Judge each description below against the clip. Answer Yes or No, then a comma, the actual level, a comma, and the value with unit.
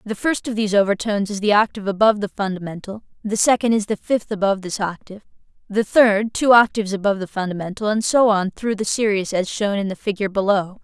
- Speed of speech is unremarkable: No, fast, 210 wpm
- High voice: Yes, high, 205 Hz